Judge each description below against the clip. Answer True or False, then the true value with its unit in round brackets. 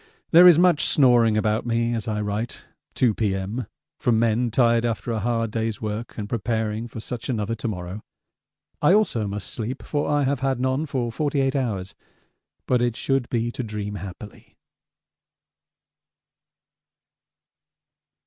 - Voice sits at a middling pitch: False (115 Hz)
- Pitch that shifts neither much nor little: True (3.2 semitones)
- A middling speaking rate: True (150 wpm)